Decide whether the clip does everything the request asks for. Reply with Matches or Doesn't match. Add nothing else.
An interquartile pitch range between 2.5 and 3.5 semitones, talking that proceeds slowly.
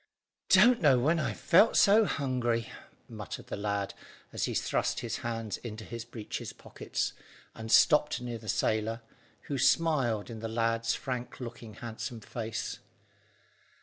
Doesn't match